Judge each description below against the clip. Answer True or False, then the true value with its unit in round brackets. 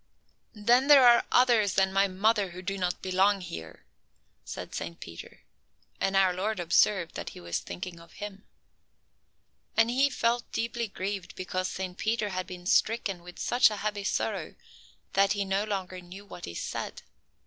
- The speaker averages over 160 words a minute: True (170 wpm)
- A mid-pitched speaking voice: False (195 Hz)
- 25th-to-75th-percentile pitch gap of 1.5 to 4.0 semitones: True (2.9 semitones)